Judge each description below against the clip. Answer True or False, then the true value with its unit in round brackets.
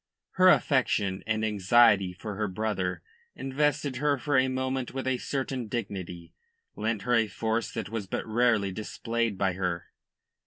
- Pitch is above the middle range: False (110 Hz)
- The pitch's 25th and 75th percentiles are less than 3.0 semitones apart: False (4.9 semitones)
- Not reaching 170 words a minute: True (155 wpm)